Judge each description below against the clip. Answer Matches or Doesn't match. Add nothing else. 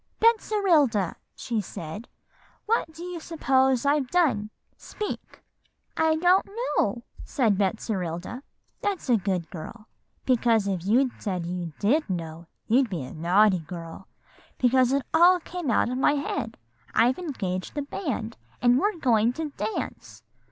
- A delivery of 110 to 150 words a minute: Matches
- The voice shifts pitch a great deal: Matches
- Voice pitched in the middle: Doesn't match